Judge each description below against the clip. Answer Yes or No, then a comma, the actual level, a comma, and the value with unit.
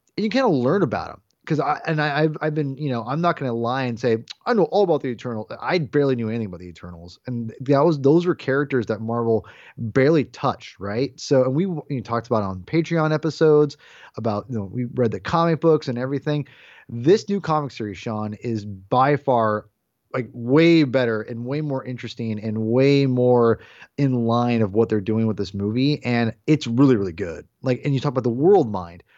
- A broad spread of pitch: No, average, 4.5 semitones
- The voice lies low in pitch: Yes, low, 125 Hz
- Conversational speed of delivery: No, fast, 215 wpm